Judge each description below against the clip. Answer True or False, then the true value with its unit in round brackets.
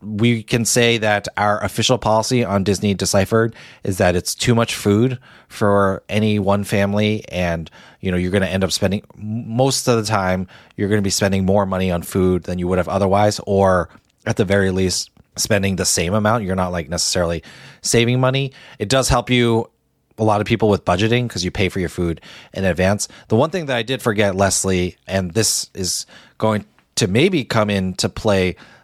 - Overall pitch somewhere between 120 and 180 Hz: False (100 Hz)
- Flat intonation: False (3.3 semitones)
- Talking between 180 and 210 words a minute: True (200 wpm)